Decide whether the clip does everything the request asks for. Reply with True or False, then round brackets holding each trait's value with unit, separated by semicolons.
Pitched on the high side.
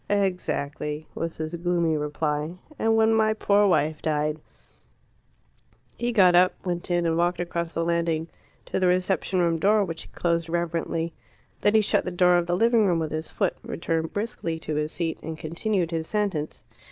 False (170 Hz)